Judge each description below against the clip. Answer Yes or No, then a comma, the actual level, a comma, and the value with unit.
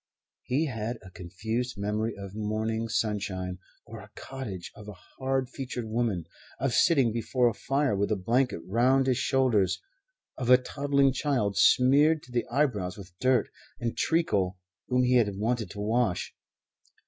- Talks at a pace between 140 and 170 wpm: Yes, average, 160 wpm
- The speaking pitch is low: Yes, low, 115 Hz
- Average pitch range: Yes, average, 4.1 semitones